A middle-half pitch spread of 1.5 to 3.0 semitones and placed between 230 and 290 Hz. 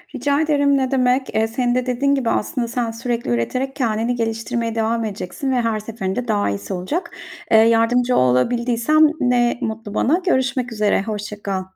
Yes: narrow, 2.6 semitones; high, 235 Hz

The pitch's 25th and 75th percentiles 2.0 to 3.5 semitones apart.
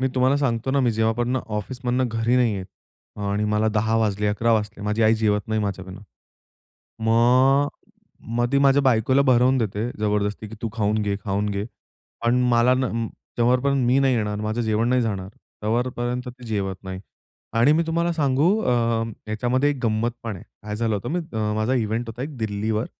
Yes: average, 3.1 semitones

